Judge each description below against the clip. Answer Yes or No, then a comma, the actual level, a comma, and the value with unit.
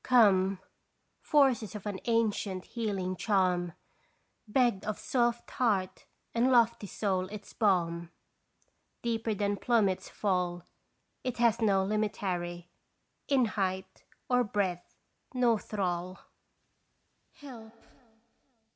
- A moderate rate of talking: No, slow, 100 wpm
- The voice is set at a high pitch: Yes, high, 205 Hz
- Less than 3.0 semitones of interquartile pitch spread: No, average, 3.8 semitones